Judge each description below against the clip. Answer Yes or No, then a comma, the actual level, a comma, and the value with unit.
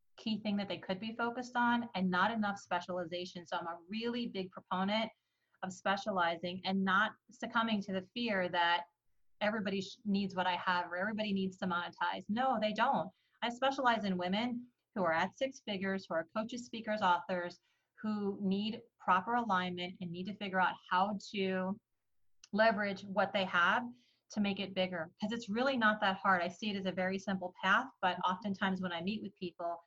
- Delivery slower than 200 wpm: Yes, average, 190 wpm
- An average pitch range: Yes, average, 3.1 semitones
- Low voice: No, high, 195 Hz